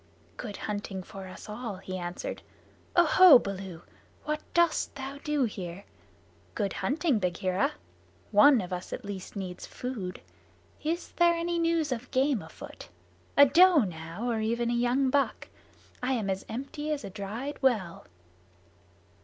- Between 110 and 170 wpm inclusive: Yes, average, 145 wpm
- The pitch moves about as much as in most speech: No, wide, 6.9 semitones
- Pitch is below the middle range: No, high, 235 Hz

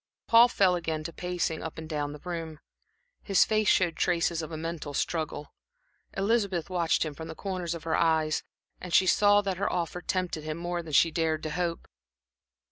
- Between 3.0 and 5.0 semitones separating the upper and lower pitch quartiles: No, narrow, 2.4 semitones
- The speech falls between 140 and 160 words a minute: No, average, 195 wpm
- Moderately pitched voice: Yes, medium, 170 Hz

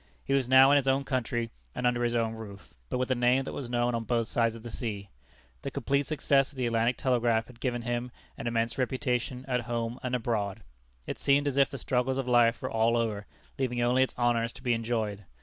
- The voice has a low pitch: Yes, low, 120 Hz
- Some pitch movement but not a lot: No, narrow, 2.0 semitones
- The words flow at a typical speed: No, fast, 235 wpm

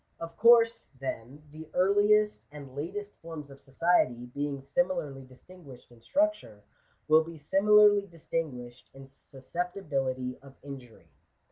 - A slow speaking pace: Yes, slow, 125 wpm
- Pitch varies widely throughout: Yes, wide, 6.5 semitones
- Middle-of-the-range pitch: Yes, medium, 150 Hz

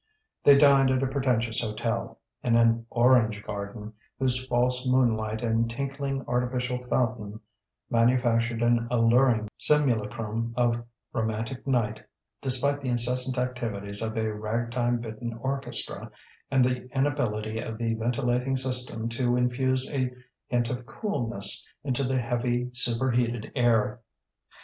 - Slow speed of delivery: Yes, slow, 125 wpm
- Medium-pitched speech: No, low, 120 Hz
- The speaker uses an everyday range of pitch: No, narrow, 2.0 semitones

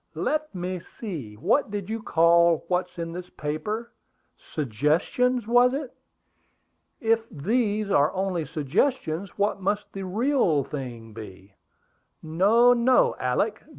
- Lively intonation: Yes, wide, 6.5 semitones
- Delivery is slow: Yes, slow, 120 wpm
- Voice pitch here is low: No, medium, 185 Hz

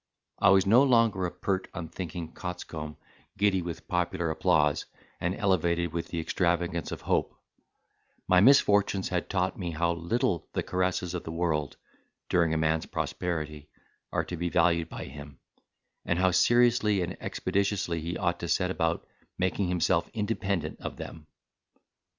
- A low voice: Yes, very low, 90 Hz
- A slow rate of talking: No, average, 150 wpm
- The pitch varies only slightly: Yes, narrow, 2.3 semitones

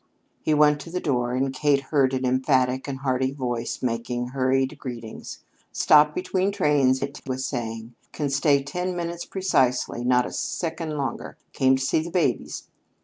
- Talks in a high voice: No, low, 135 Hz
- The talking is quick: No, average, 165 wpm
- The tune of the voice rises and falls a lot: No, average, 3.0 semitones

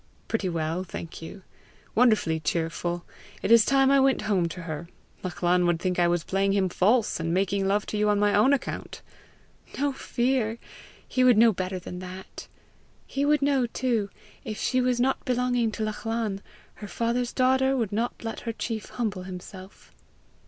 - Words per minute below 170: No, average, 175 wpm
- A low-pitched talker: No, high, 210 Hz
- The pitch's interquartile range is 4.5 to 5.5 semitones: Yes, average, 5.1 semitones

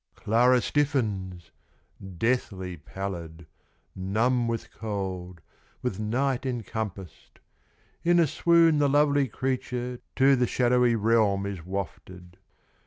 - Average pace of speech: No, slow, 105 wpm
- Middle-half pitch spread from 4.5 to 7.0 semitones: Yes, average, 5.2 semitones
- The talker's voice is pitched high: No, low, 115 Hz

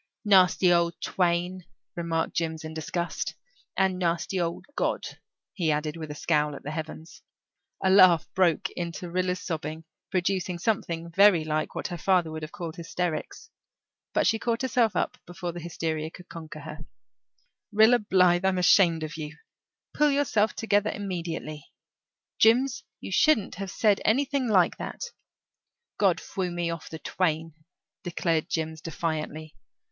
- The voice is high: No, medium, 175 Hz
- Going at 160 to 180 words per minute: No, average, 150 wpm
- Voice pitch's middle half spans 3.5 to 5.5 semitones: No, average, 3.1 semitones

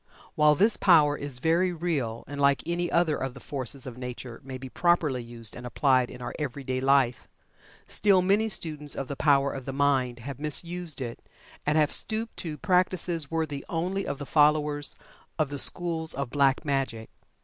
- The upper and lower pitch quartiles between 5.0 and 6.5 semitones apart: No, average, 3.9 semitones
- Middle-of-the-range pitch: Yes, medium, 145 Hz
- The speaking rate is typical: Yes, average, 185 wpm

